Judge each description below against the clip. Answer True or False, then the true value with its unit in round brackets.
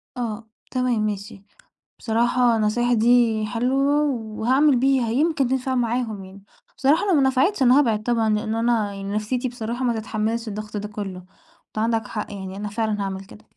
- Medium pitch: False (230 Hz)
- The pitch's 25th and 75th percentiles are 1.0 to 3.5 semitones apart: True (3.0 semitones)